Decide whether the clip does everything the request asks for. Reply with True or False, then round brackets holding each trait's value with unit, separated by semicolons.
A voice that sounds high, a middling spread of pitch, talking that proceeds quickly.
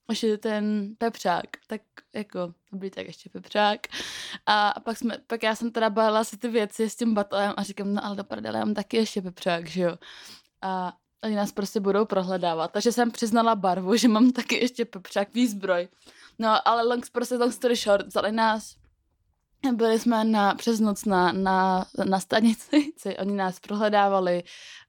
True (210 Hz; 3.0 semitones; 175 wpm)